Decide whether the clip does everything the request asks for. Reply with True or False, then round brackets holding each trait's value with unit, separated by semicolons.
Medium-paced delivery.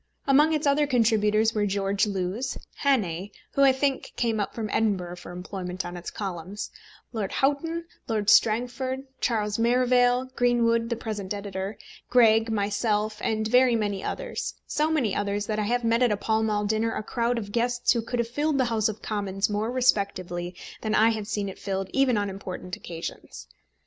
True (180 wpm)